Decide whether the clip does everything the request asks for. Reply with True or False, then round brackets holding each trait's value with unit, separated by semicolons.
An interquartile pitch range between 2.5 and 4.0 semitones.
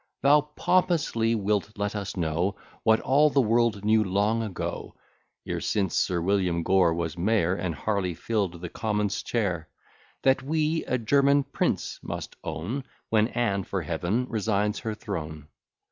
False (4.5 semitones)